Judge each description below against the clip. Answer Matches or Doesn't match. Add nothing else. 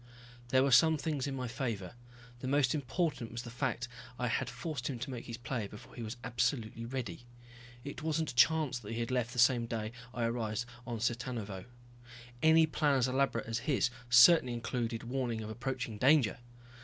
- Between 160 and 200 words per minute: Matches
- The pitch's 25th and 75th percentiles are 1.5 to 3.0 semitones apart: Matches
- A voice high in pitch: Doesn't match